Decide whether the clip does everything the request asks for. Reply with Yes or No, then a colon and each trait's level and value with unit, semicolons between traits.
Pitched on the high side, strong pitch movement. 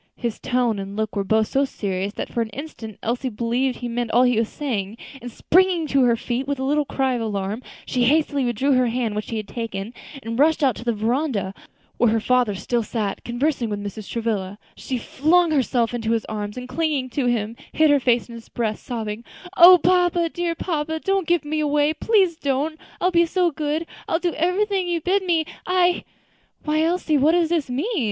Yes: very high, 255 Hz; wide, 5.7 semitones